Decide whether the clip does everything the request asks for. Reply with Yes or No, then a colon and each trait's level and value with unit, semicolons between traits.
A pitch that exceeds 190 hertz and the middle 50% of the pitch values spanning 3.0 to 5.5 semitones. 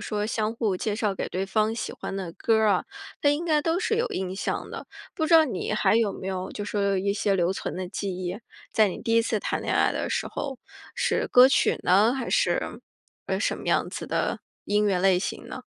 Yes: high, 210 Hz; average, 3.5 semitones